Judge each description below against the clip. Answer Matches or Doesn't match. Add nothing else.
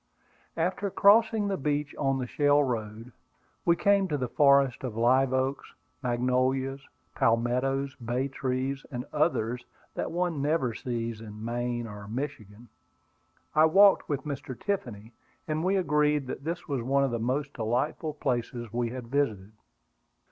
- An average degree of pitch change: Matches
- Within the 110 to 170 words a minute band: Matches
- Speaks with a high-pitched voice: Doesn't match